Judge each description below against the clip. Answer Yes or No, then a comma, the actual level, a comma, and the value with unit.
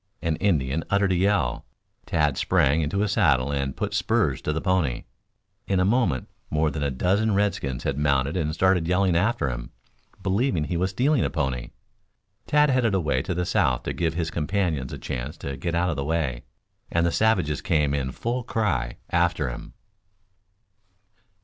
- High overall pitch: No, very low, 80 Hz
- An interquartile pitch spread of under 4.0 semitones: No, wide, 5.5 semitones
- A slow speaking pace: No, average, 180 wpm